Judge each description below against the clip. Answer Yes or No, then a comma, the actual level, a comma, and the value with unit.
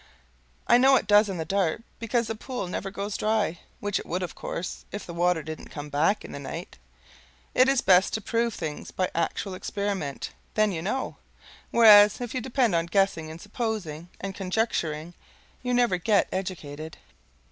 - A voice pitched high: Yes, high, 195 Hz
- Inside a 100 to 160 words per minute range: No, average, 180 wpm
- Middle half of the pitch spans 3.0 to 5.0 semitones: Yes, average, 4.7 semitones